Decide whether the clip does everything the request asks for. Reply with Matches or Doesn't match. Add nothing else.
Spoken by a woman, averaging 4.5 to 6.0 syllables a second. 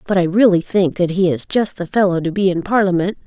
Matches